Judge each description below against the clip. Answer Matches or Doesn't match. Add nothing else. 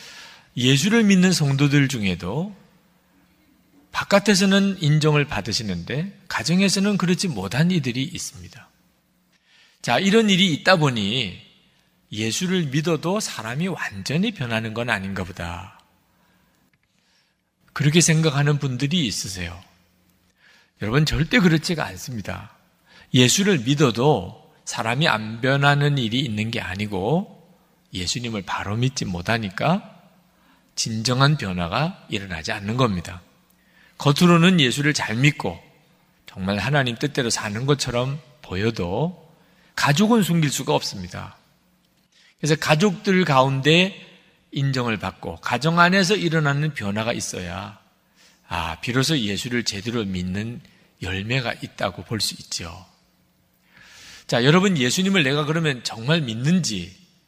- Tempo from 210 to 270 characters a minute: Matches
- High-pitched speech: Doesn't match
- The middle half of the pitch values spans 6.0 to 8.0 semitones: Matches